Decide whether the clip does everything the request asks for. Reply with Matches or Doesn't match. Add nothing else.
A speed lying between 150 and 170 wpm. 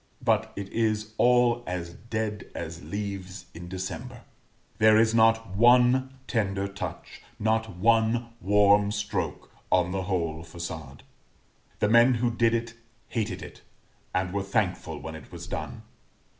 Doesn't match